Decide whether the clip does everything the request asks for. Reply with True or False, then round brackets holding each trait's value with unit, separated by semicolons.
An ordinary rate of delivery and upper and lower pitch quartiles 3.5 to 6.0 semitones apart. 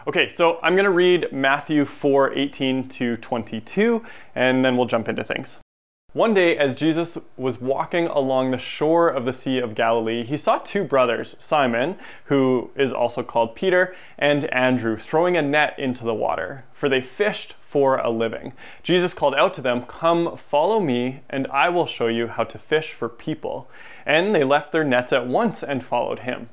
True (185 wpm; 4.8 semitones)